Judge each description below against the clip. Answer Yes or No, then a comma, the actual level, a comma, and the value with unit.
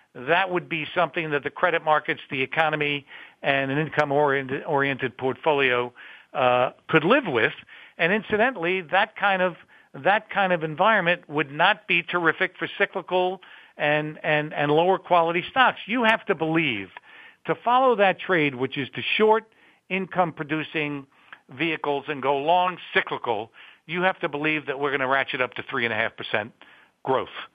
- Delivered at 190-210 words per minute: No, average, 160 wpm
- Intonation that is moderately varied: Yes, average, 4.3 semitones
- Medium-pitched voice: Yes, medium, 160 Hz